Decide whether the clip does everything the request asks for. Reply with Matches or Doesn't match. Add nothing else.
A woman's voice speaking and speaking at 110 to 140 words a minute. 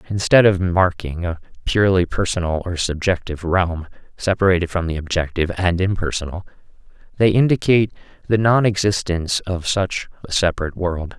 Doesn't match